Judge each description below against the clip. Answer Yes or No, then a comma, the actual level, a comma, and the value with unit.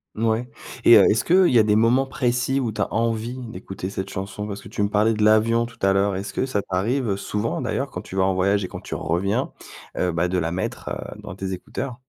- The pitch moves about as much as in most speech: Yes, average, 3.5 semitones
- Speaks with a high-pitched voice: No, low, 105 Hz